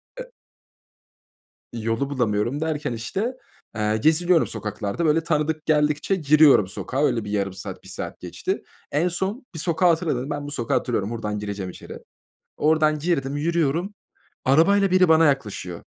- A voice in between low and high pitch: Yes, medium, 150 Hz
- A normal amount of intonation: No, wide, 6.3 semitones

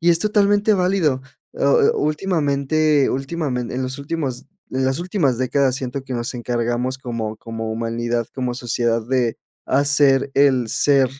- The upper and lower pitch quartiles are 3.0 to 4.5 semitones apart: Yes, average, 3.7 semitones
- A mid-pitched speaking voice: No, low, 130 Hz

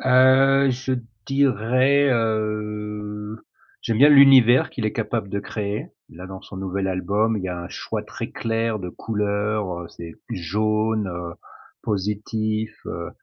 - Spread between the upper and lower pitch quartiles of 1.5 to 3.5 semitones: Yes, average, 2.7 semitones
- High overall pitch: No, low, 110 Hz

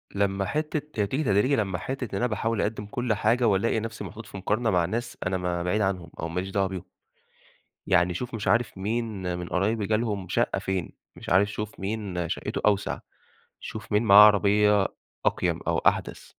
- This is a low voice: Yes, low, 105 Hz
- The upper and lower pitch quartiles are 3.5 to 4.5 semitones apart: No, average, 2.8 semitones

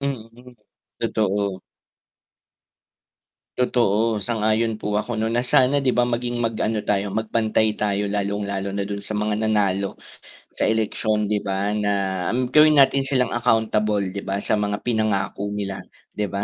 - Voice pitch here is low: Yes, low, 105 Hz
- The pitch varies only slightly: Yes, narrow, 2.2 semitones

